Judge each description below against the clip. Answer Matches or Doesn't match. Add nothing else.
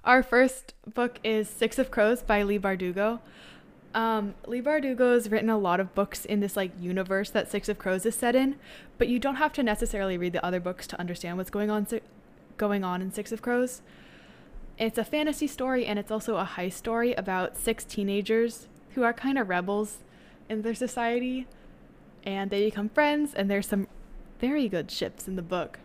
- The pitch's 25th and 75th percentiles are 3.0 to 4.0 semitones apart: Matches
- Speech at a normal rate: Matches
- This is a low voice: Doesn't match